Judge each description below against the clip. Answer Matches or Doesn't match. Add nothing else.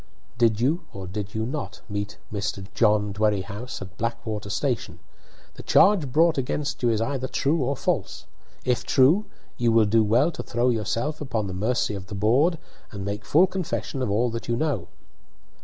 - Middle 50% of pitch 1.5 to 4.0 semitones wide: Doesn't match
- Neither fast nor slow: Matches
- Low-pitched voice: Matches